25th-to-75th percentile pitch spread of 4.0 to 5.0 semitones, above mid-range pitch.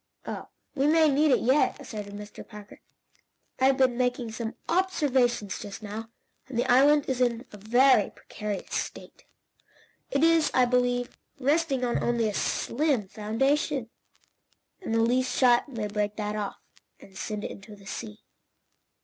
Yes: average, 4.3 semitones; high, 245 Hz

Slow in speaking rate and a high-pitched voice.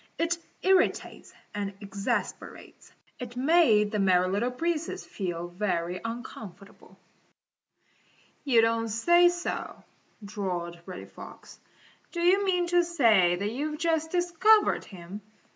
Yes: slow, 115 wpm; high, 230 Hz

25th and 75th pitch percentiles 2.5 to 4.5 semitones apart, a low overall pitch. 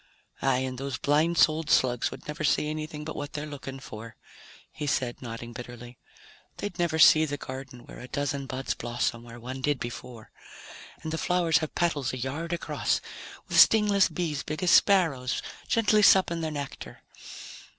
No: average, 4.1 semitones; medium, 145 Hz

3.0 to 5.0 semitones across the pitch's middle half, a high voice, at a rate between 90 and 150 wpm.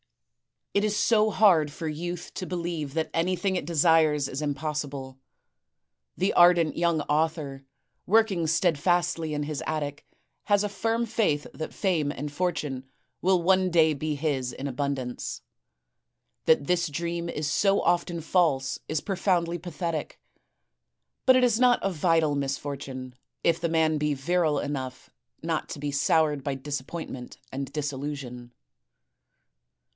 No: average, 3.5 semitones; medium, 160 Hz; average, 140 wpm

